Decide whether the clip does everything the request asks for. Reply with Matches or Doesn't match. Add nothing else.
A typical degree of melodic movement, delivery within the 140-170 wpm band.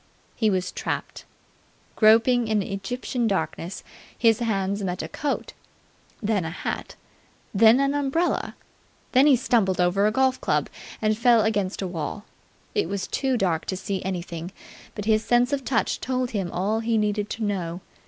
Matches